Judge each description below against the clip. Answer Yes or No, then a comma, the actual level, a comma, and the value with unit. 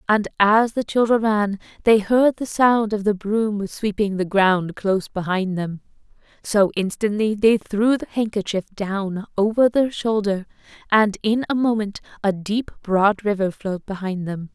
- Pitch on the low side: No, high, 205 Hz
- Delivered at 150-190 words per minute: Yes, average, 160 wpm